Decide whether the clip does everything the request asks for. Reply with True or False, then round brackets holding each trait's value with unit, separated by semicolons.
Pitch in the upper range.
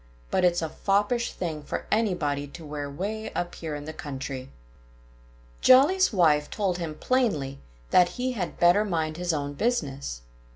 False (170 Hz)